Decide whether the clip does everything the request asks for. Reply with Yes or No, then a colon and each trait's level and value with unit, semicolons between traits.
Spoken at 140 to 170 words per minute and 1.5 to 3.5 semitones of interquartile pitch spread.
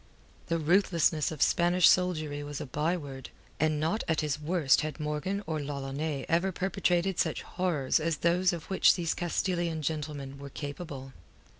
Yes: average, 155 wpm; average, 3.1 semitones